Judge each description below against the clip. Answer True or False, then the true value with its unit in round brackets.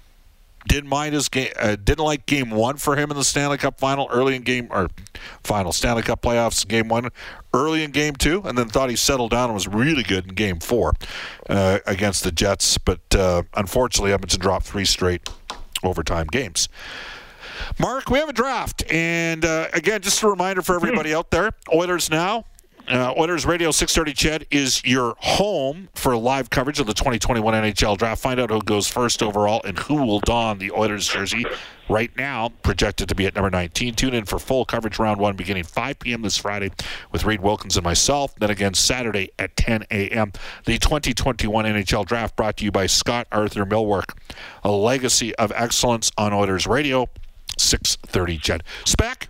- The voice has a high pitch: False (115 Hz)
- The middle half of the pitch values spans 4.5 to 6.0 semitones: True (5.3 semitones)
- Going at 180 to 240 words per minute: True (190 wpm)